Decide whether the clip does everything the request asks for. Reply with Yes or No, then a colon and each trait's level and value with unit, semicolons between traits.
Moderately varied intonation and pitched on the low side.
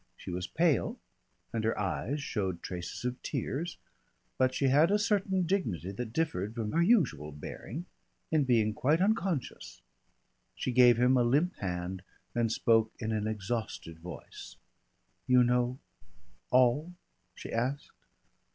No: wide, 6.0 semitones; low, 125 Hz